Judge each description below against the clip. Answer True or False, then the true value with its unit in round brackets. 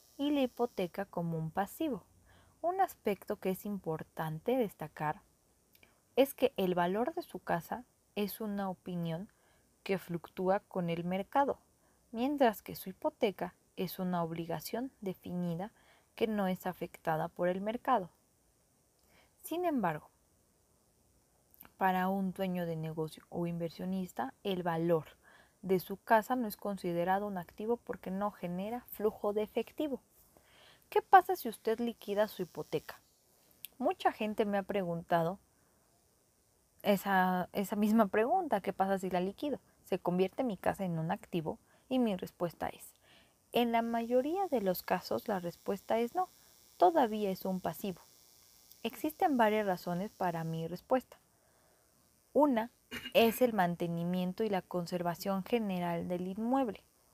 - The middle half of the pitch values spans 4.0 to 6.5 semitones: True (4.6 semitones)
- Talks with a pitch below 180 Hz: False (195 Hz)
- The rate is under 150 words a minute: True (135 wpm)